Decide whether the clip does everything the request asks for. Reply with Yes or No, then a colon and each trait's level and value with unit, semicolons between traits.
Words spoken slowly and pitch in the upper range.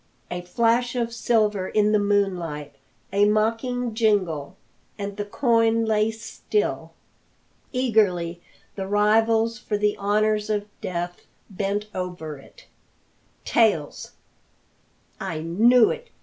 Yes: slow, 110 wpm; high, 210 Hz